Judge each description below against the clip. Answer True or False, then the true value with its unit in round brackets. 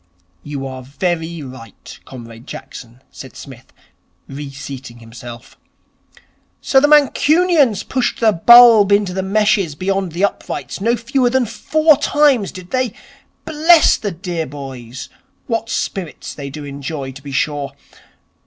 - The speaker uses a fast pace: False (135 wpm)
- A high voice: False (175 Hz)